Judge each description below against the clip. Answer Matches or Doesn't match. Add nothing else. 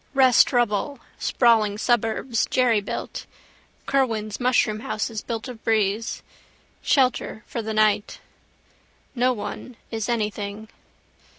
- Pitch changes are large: Doesn't match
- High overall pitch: Matches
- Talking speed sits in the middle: Doesn't match